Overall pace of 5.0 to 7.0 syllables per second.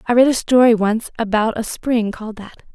Yes: 5.3 syllables/s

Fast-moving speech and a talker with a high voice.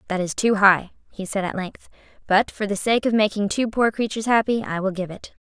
Yes: fast, 245 wpm; high, 205 Hz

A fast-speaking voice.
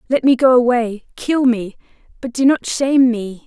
No: average, 190 wpm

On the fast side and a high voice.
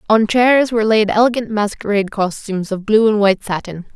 No: average, 180 wpm; high, 210 Hz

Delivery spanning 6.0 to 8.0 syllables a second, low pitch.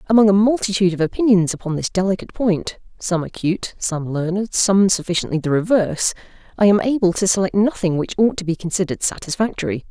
No: 6.3 syllables/s; high, 190 Hz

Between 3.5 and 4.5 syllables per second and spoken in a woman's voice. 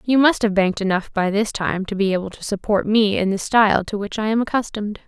No: 6.1 syllables/s; female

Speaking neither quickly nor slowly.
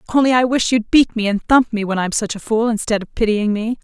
No: fast, 280 wpm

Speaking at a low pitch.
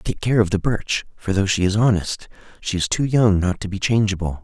Yes: low, 100 Hz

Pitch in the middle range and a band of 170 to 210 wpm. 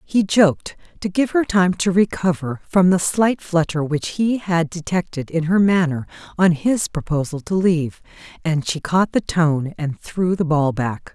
Yes: medium, 170 Hz; average, 185 wpm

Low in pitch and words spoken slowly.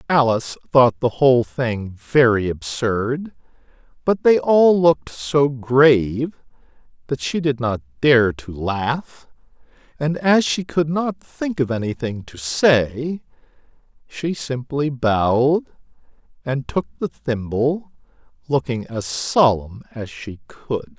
Yes: low, 130 Hz; slow, 125 wpm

